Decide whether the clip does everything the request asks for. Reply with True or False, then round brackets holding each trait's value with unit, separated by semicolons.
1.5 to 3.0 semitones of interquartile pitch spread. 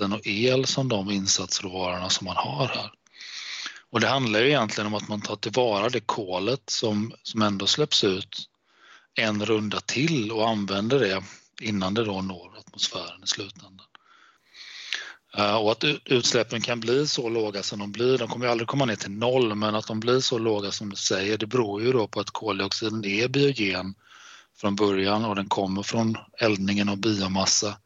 True (2.6 semitones)